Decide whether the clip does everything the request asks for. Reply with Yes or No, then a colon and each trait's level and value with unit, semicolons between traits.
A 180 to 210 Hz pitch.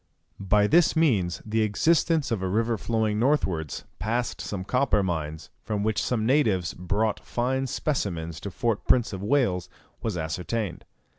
No: low, 110 Hz